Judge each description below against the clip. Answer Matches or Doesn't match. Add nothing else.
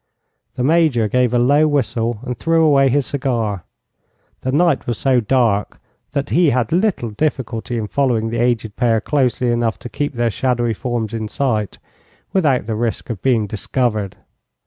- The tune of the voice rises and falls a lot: Doesn't match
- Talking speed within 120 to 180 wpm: Matches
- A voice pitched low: Matches